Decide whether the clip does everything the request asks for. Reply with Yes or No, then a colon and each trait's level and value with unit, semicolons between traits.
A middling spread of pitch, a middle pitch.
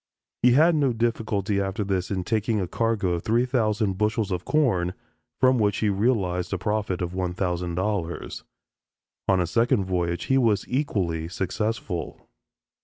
No: average, 4.0 semitones; low, 100 Hz